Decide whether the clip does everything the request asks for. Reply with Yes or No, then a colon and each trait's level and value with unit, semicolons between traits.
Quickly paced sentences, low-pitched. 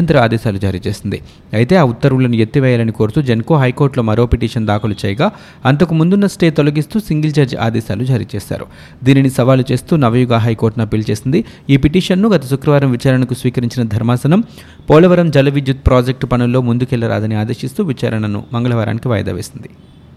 Yes: fast, 140 wpm; low, 125 Hz